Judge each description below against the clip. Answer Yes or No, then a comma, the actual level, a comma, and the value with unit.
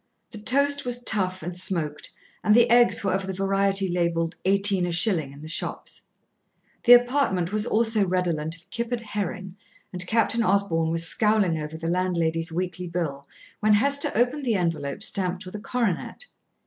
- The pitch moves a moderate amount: Yes, average, 4.5 semitones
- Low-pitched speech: No, high, 190 Hz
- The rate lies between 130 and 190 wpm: Yes, average, 170 wpm